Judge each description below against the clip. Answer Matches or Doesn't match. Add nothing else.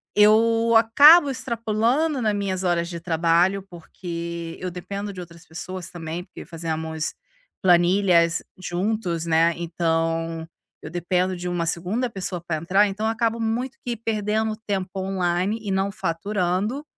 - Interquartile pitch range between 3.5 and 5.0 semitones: Matches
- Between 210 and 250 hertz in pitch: Doesn't match